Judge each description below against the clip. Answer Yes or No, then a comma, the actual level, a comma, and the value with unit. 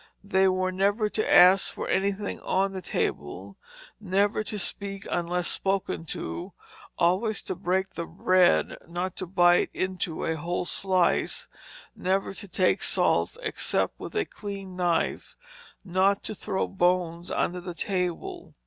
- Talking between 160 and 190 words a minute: No, average, 140 wpm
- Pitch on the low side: No, medium, 185 Hz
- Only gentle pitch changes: Yes, narrow, 1.9 semitones